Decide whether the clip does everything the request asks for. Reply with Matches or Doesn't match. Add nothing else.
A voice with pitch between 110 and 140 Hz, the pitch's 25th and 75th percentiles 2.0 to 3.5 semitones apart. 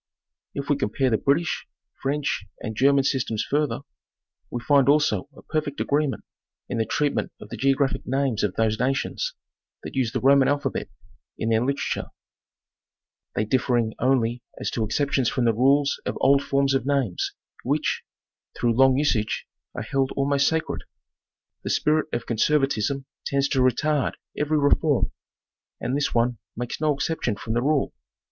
Matches